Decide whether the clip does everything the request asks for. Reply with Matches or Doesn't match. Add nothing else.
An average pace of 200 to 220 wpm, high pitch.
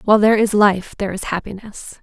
Matches